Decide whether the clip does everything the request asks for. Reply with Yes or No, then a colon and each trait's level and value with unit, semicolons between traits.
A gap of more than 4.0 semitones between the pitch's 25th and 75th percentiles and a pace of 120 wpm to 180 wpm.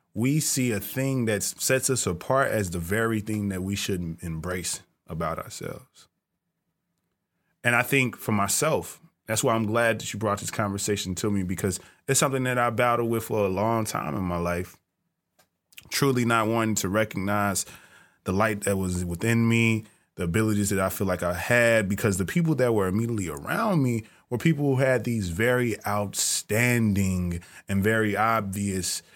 No: average, 3.7 semitones; average, 175 wpm